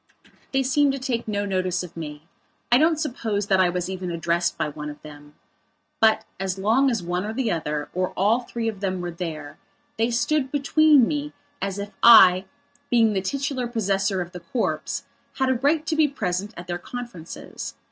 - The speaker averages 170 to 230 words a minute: Yes, average, 195 wpm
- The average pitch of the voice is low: No, high, 200 Hz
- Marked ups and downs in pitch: Yes, wide, 6.0 semitones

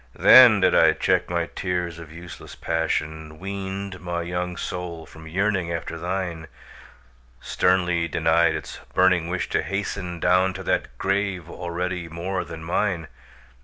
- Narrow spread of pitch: Yes, narrow, 2.1 semitones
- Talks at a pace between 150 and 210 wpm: No, average, 140 wpm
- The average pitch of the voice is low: Yes, very low, 90 Hz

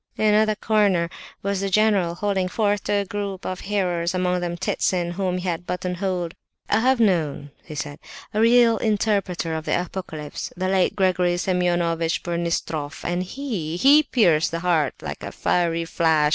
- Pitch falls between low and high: Yes, medium, 180 Hz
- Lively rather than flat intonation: No, average, 3.2 semitones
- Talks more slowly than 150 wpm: No, average, 165 wpm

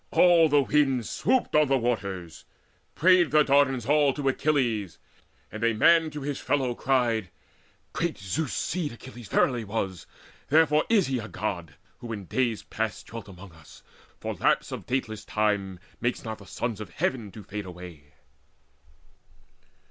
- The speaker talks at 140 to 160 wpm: Yes, average, 155 wpm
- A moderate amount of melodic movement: No, wide, 5.8 semitones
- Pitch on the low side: Yes, low, 120 Hz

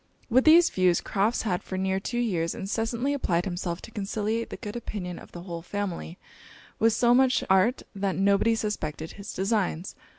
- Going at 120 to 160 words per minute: No, average, 175 wpm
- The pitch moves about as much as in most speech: Yes, average, 3.9 semitones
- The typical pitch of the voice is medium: No, high, 200 Hz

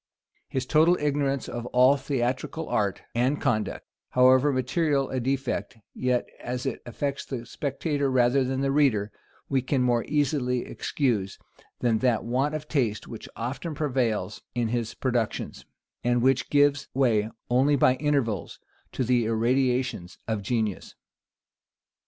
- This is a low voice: Yes, low, 130 Hz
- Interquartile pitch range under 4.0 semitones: Yes, average, 2.8 semitones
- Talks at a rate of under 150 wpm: Yes, average, 140 wpm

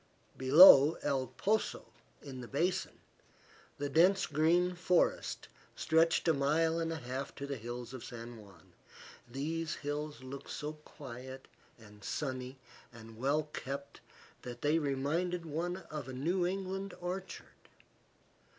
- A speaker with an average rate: No, slow, 130 wpm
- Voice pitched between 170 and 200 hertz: No, medium, 145 Hz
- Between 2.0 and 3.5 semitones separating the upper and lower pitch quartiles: No, average, 4.3 semitones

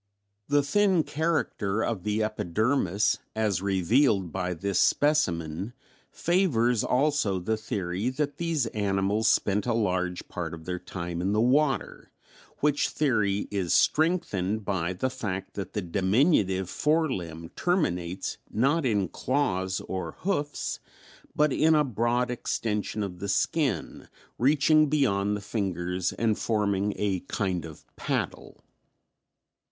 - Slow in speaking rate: Yes, slow, 130 wpm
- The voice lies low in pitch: Yes, low, 105 Hz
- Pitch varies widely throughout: Yes, wide, 6.6 semitones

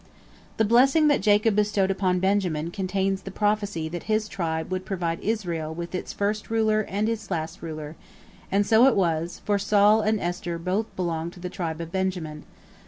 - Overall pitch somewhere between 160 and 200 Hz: Yes, high, 190 Hz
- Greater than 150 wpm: Yes, average, 180 wpm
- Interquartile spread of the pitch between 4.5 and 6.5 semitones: No, average, 3.7 semitones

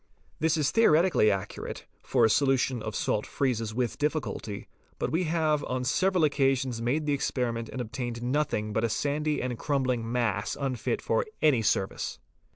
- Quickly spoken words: No, average, 165 wpm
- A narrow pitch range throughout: No, average, 4.5 semitones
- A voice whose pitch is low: Yes, low, 130 Hz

